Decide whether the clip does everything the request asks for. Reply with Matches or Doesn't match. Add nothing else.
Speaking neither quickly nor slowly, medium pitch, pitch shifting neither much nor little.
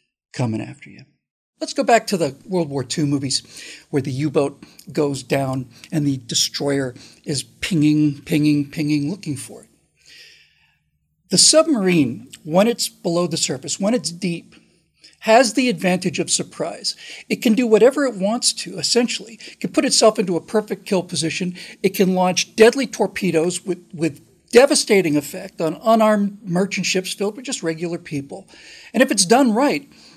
Doesn't match